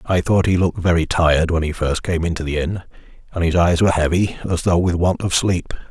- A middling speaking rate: No, fast, 245 wpm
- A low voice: Yes, very low, 85 Hz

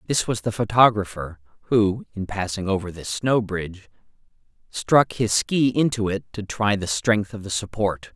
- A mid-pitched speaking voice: No, low, 105 Hz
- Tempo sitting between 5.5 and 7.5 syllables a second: No, 4.6 syllables/s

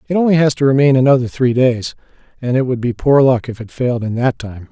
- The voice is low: Yes, low, 130 Hz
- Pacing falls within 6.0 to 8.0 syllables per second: Yes, 6.1 syllables/s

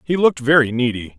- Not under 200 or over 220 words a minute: Yes, fast, 205 wpm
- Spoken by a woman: No, male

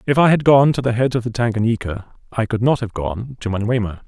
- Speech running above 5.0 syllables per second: Yes, 6.0 syllables/s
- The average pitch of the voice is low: Yes, low, 115 Hz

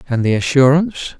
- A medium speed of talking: Yes, average, 150 wpm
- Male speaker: Yes, male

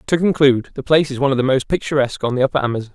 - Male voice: Yes, male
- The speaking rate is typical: No, fast, 285 wpm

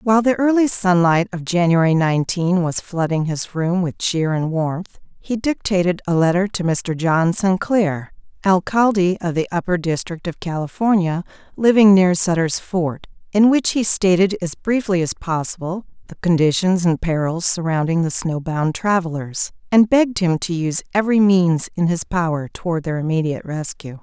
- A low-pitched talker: No, medium, 175 Hz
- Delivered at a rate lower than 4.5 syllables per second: No, 4.9 syllables/s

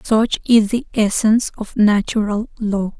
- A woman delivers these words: Yes, female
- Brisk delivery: No, average, 140 wpm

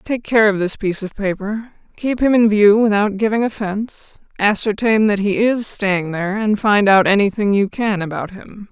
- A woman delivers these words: Yes, female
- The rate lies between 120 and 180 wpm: No, average, 195 wpm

